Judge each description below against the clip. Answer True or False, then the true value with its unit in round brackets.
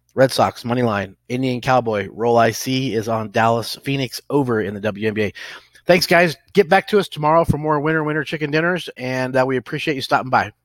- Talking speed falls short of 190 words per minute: False (205 wpm)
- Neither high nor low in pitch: False (130 Hz)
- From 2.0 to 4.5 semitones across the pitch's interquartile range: False (5.1 semitones)